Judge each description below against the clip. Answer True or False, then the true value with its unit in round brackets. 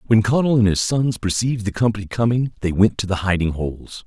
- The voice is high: False (105 Hz)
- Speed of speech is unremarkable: False (220 wpm)